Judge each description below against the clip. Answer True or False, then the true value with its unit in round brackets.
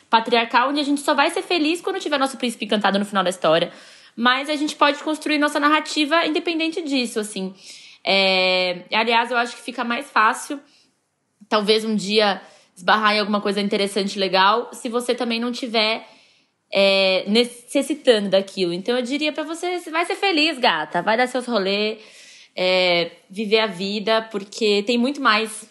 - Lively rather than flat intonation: True (5.9 semitones)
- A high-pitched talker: True (230 Hz)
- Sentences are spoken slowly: False (175 wpm)